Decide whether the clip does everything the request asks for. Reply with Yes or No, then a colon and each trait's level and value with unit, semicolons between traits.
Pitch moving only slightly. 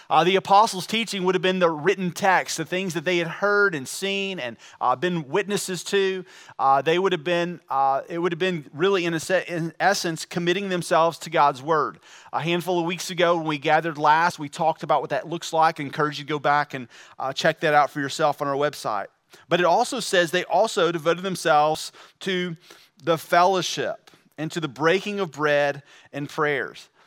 No: average, 3.3 semitones